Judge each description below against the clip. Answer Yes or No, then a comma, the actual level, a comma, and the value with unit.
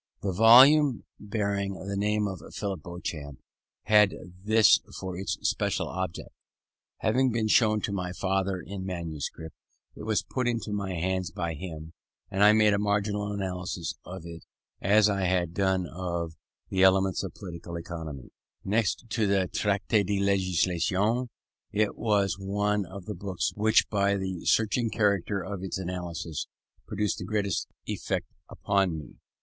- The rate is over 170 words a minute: No, average, 150 wpm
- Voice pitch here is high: No, very low, 95 Hz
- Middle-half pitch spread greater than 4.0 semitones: No, narrow, 2.6 semitones